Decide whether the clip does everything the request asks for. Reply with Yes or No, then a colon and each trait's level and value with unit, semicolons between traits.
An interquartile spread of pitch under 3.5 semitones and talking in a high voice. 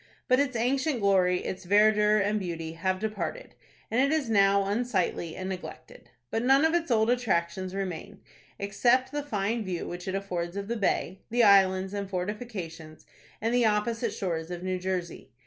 No: average, 4.0 semitones; high, 200 Hz